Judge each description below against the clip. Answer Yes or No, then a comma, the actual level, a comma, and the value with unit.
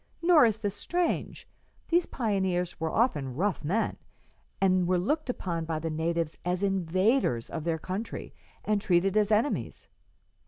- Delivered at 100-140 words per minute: No, average, 150 wpm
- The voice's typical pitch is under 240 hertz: Yes, high, 190 Hz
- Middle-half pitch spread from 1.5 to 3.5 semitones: No, average, 4.6 semitones